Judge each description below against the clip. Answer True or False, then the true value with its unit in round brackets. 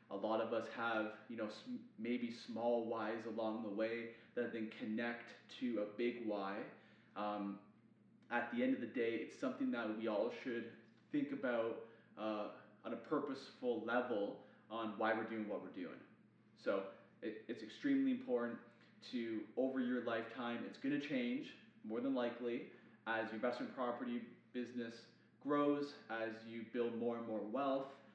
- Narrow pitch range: True (2.0 semitones)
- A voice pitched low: True (115 Hz)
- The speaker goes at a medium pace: True (160 wpm)